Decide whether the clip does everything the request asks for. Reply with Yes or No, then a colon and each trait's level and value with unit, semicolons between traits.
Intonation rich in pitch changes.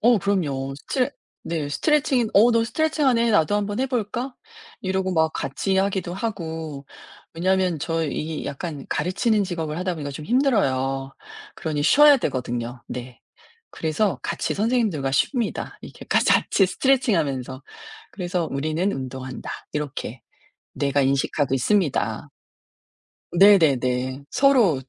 Yes: wide, 7.4 semitones